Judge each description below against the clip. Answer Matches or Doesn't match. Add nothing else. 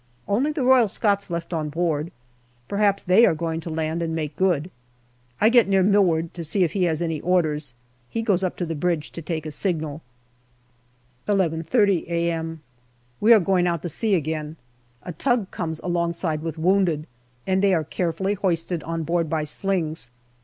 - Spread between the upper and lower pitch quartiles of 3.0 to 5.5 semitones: Matches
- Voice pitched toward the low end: Doesn't match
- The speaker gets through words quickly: Doesn't match